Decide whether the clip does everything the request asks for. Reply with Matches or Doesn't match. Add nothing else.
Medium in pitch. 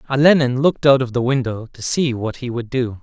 Doesn't match